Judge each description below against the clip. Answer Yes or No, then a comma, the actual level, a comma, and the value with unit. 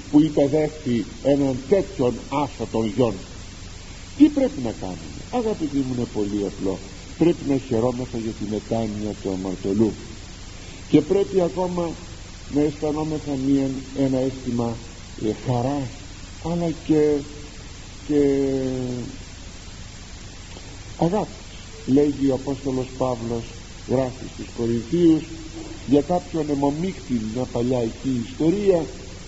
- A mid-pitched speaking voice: No, low, 125 Hz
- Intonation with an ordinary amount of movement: No, wide, 6.4 semitones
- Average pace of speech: No, slow, 105 wpm